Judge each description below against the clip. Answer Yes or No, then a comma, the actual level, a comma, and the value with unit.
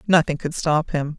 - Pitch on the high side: No, medium, 160 Hz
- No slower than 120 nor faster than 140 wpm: No, average, 200 wpm